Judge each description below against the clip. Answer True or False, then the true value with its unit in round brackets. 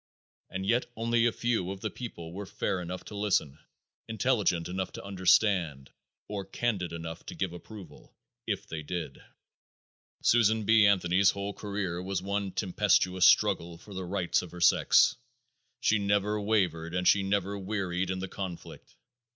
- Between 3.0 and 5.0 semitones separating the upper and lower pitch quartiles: False (2.6 semitones)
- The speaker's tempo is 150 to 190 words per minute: True (160 wpm)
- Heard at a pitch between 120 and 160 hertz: False (95 Hz)